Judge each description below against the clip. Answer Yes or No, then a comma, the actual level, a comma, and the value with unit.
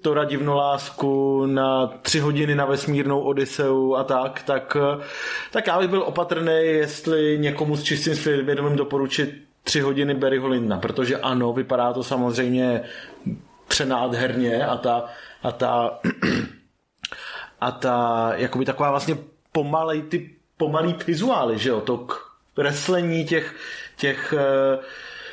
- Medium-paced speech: Yes, average, 125 wpm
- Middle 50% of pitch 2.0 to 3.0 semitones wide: Yes, average, 2.7 semitones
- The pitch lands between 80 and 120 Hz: No, medium, 140 Hz